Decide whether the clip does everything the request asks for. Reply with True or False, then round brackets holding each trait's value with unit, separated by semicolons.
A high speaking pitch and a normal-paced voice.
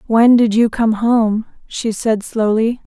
True (225 Hz; 160 wpm)